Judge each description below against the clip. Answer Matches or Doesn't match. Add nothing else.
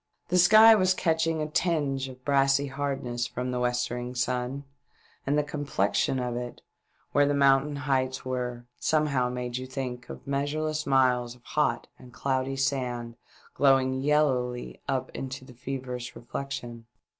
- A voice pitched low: Matches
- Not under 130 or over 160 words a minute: Matches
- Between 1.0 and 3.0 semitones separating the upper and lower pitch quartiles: Matches